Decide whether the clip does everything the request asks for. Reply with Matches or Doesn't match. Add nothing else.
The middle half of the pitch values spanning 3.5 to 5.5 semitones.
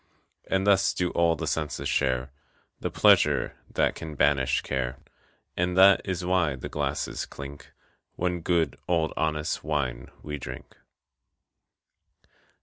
Matches